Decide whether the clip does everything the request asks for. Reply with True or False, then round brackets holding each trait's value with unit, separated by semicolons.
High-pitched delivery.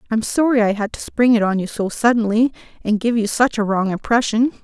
True (225 Hz)